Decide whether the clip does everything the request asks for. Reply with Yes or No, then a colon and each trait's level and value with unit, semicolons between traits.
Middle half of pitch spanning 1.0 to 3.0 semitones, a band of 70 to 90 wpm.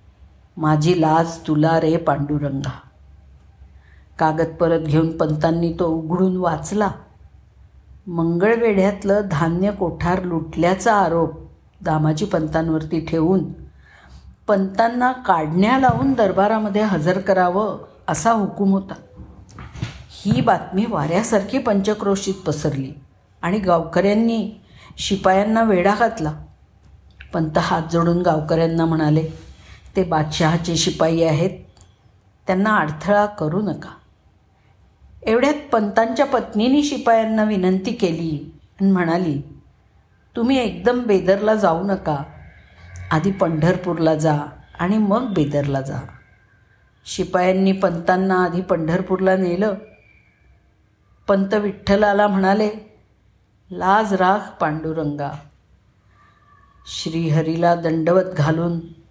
No: average, 4.6 semitones; average, 85 wpm